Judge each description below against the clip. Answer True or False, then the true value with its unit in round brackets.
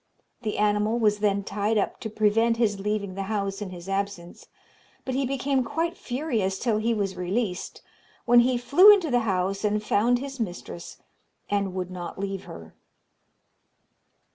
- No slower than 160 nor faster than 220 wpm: True (165 wpm)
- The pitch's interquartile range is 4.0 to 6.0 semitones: False (3.6 semitones)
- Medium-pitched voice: False (210 Hz)